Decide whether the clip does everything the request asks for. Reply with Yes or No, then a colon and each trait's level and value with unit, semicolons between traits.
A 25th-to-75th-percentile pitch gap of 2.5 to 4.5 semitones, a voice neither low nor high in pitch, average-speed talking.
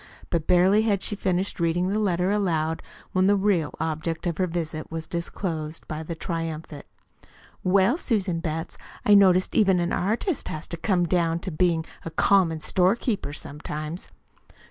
Yes: average, 3.0 semitones; medium, 175 Hz; average, 160 wpm